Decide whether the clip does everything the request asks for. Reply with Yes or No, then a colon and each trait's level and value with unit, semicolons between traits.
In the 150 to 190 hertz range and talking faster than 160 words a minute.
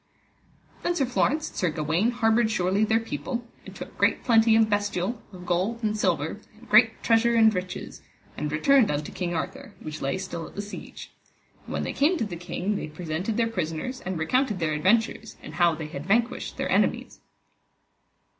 No: high, 205 Hz; average, 190 wpm